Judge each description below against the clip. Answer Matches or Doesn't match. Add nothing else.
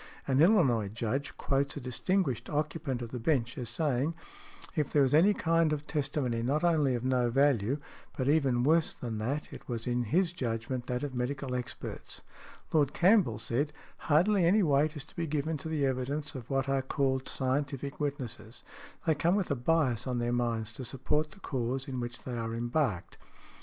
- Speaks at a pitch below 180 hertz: Matches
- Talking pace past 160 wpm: Matches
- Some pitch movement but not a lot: Matches